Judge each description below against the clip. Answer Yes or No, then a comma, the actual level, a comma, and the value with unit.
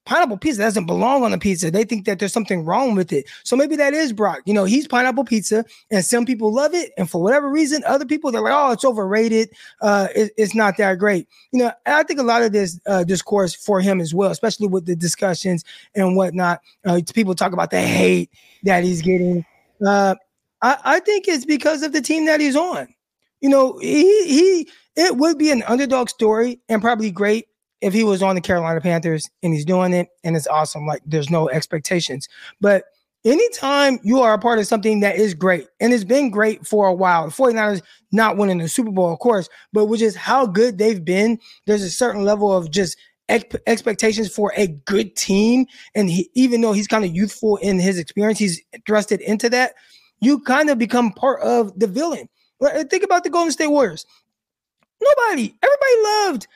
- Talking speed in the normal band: No, fast, 210 wpm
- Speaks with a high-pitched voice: Yes, high, 215 Hz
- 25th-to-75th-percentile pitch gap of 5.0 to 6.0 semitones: Yes, average, 5.3 semitones